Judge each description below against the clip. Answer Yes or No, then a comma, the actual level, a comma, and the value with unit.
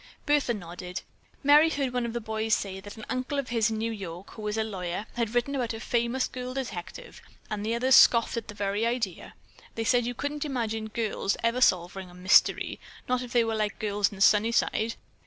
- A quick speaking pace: Yes, fast, 215 wpm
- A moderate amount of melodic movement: Yes, average, 3.2 semitones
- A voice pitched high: Yes, high, 225 Hz